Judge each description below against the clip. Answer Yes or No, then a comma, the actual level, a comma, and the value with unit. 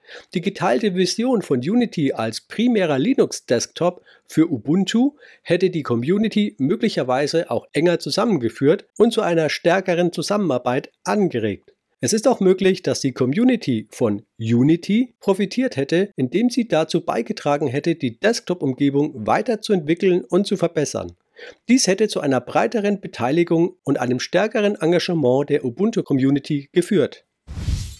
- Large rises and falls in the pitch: Yes, wide, 6.8 semitones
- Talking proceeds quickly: No, slow, 125 wpm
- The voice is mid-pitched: Yes, medium, 175 Hz